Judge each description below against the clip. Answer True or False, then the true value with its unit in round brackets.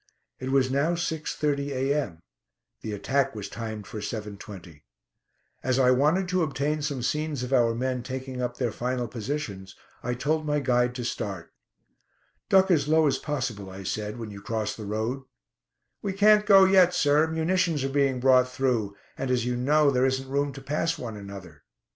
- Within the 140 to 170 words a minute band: False (180 wpm)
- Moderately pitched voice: False (130 Hz)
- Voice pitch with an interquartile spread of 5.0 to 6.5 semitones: False (4.6 semitones)